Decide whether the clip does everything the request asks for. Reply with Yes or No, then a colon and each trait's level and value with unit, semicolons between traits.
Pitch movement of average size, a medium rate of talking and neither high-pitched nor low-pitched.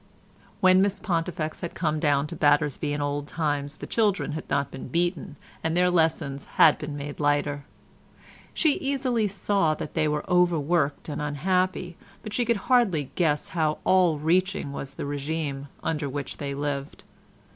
Yes: average, 3.9 semitones; average, 165 wpm; medium, 155 Hz